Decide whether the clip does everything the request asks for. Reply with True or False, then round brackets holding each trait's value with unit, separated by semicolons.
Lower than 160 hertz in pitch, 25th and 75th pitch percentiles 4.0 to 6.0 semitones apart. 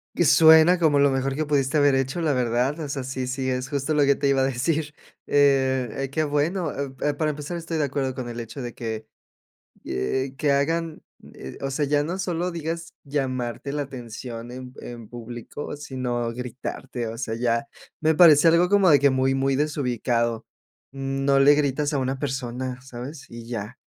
False (135 Hz; 2.9 semitones)